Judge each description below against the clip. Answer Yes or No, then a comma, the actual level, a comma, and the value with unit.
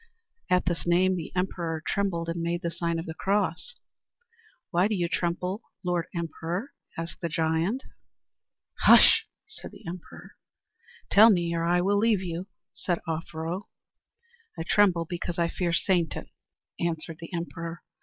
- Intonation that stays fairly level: Yes, narrow, 2.0 semitones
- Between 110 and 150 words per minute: Yes, average, 145 wpm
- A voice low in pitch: No, medium, 175 Hz